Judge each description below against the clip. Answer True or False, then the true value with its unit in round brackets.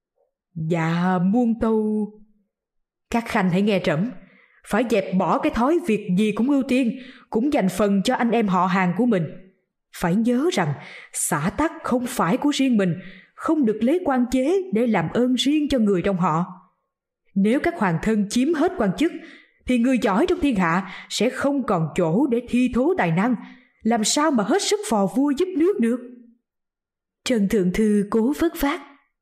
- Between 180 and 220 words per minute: True (185 wpm)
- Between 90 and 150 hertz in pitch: False (235 Hz)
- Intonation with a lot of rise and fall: True (5.7 semitones)